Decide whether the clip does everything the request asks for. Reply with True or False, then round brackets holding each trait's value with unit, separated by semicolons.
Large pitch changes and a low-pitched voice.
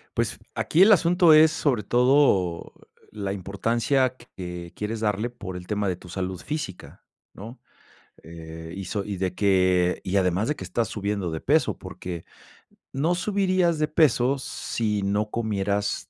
True (6.5 semitones; 105 Hz)